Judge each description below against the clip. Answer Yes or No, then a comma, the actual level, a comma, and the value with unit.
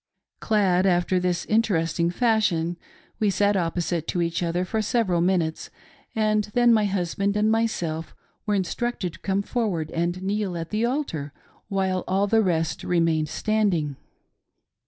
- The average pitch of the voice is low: No, medium, 185 Hz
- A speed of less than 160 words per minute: Yes, average, 145 wpm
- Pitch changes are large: No, average, 4.0 semitones